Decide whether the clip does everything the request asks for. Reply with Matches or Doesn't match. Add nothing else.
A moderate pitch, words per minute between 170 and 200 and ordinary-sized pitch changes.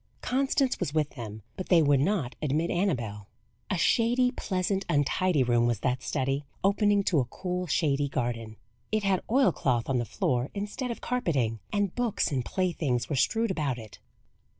Doesn't match